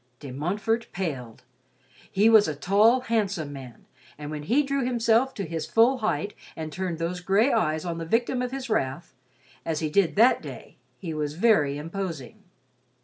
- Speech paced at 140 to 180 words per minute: Yes, average, 175 wpm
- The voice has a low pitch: No, high, 190 Hz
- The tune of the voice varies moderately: No, wide, 6.7 semitones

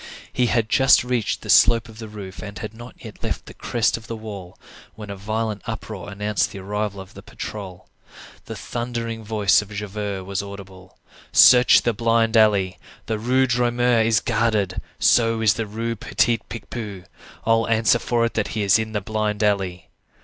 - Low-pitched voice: Yes, low, 110 Hz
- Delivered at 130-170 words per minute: No, average, 185 wpm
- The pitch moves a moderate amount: No, narrow, 2.3 semitones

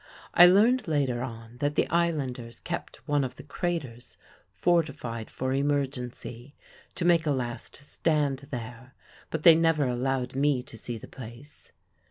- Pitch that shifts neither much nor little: Yes, average, 4.1 semitones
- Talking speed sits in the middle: Yes, average, 150 wpm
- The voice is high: No, low, 135 Hz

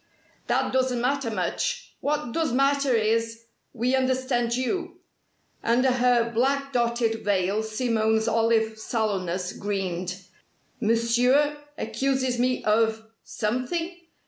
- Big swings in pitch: No, average, 2.9 semitones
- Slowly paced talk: Yes, slow, 105 wpm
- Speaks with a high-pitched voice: Yes, high, 235 Hz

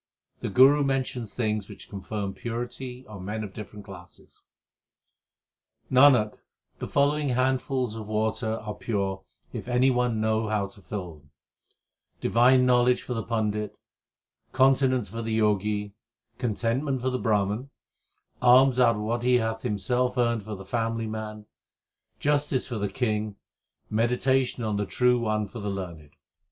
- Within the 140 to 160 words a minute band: Yes, average, 150 wpm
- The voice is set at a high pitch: No, low, 115 Hz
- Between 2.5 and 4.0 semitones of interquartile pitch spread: Yes, average, 3.1 semitones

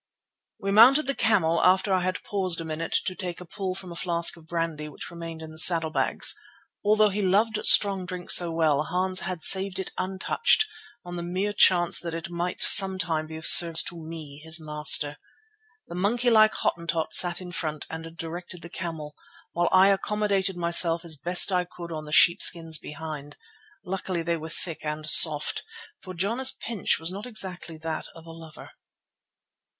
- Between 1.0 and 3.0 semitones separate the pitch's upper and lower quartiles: Yes, average, 2.7 semitones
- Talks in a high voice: No, medium, 175 Hz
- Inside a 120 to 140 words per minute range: No, average, 185 wpm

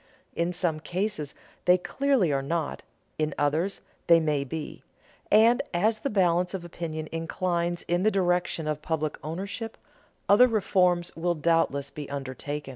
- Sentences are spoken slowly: No, average, 145 wpm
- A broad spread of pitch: No, average, 3.4 semitones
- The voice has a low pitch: No, medium, 170 Hz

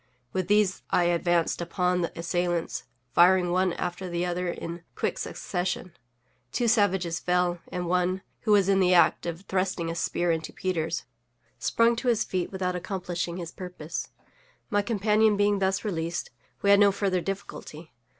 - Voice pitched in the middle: Yes, medium, 180 Hz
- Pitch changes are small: Yes, narrow, 2.2 semitones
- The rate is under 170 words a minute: Yes, average, 160 wpm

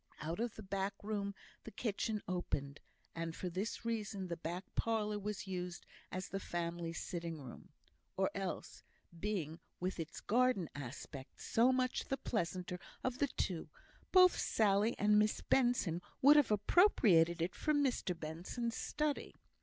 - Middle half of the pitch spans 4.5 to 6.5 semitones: Yes, average, 5.1 semitones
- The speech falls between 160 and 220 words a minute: No, average, 150 wpm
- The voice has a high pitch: Yes, high, 195 Hz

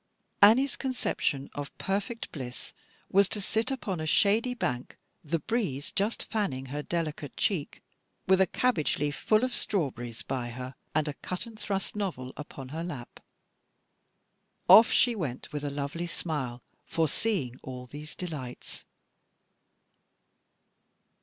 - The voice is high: No, medium, 160 Hz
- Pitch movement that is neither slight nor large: No, wide, 7.3 semitones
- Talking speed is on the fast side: No, slow, 135 wpm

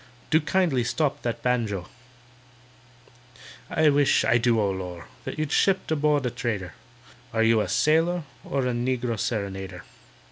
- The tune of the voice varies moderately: No, wide, 5.7 semitones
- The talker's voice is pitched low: Yes, low, 120 Hz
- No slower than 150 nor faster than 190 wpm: No, slow, 135 wpm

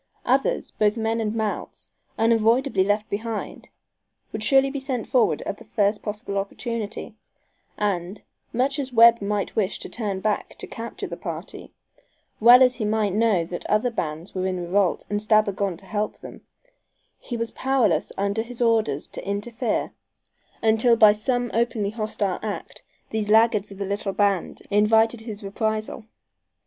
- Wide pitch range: No, narrow, 2.4 semitones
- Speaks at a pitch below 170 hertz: No, high, 215 Hz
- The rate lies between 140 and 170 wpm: Yes, average, 160 wpm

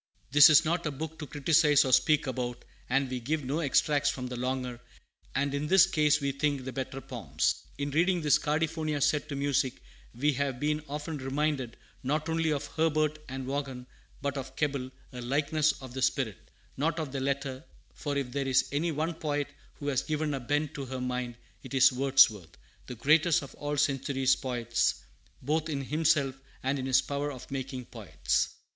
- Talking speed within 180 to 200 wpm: Yes, average, 190 wpm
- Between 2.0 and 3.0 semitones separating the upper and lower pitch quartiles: Yes, narrow, 2.5 semitones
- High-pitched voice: No, medium, 140 Hz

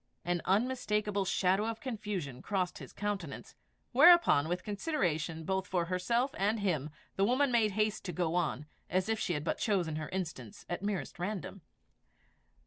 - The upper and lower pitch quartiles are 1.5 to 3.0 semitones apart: No, average, 3.6 semitones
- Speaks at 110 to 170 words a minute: Yes, average, 160 wpm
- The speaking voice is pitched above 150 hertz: Yes, high, 190 Hz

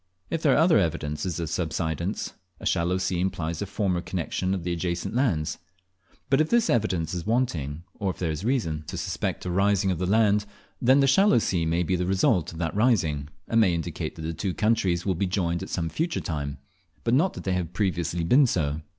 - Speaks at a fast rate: Yes, fast, 220 wpm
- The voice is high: No, very low, 90 Hz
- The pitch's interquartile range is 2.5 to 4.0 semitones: No, average, 4.5 semitones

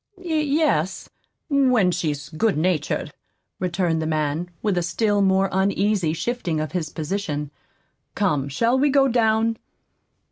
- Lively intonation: Yes, wide, 6.3 semitones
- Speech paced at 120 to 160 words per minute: Yes, slow, 135 wpm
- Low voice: No, high, 190 Hz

